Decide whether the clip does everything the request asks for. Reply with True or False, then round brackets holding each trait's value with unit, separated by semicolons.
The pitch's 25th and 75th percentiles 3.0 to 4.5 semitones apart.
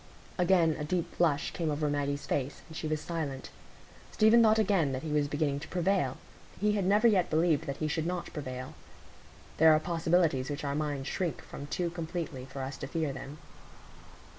True (3.7 semitones)